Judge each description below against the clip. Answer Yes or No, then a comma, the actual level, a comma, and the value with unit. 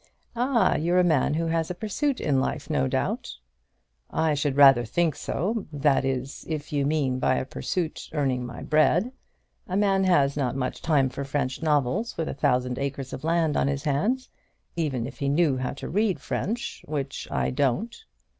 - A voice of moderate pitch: Yes, medium, 145 Hz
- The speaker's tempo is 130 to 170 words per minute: No, average, 185 wpm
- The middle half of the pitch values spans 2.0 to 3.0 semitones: No, average, 4.4 semitones